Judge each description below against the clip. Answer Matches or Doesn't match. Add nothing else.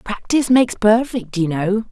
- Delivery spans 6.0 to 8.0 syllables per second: Doesn't match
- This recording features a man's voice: Doesn't match